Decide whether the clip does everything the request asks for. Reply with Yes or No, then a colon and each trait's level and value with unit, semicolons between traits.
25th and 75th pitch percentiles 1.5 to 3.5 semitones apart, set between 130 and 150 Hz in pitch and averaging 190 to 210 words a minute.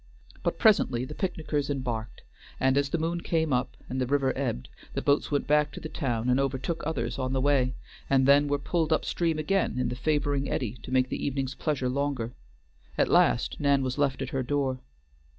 Yes: narrow, 2.4 semitones; low, 135 Hz; fast, 205 wpm